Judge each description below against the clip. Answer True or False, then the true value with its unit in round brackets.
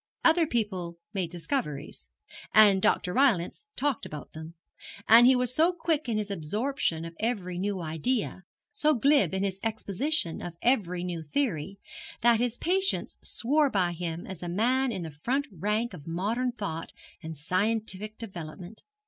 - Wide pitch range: True (6.3 semitones)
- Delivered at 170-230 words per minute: False (155 wpm)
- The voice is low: False (205 Hz)